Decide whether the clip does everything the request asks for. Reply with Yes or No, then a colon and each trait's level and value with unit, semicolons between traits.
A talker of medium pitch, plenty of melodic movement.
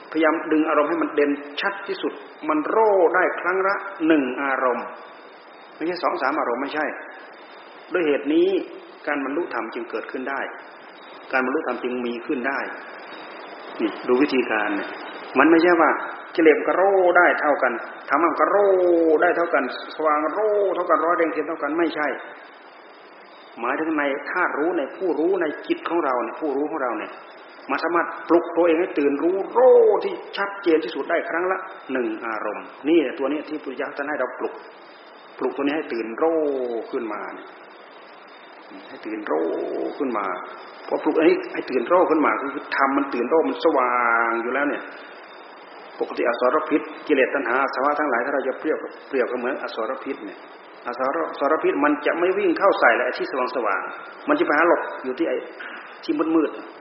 Yes: medium, 165 Hz; wide, 5.9 semitones